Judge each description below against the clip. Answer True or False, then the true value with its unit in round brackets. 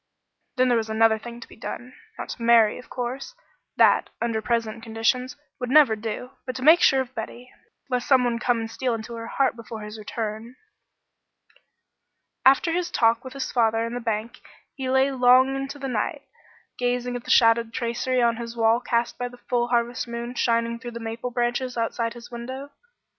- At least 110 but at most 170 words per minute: False (195 wpm)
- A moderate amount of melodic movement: False (1.8 semitones)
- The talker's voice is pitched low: False (240 Hz)